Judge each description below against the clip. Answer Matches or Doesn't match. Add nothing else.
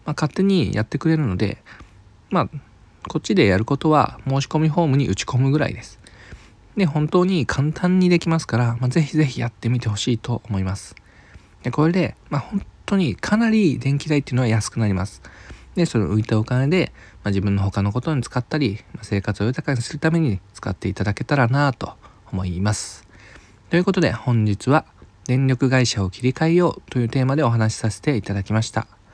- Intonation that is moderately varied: Doesn't match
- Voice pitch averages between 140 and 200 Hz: Doesn't match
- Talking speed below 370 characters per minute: Doesn't match